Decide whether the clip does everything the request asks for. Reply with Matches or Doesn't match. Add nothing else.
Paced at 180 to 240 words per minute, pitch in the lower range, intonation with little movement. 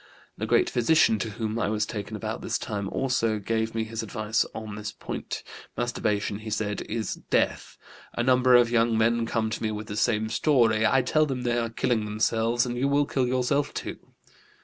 Matches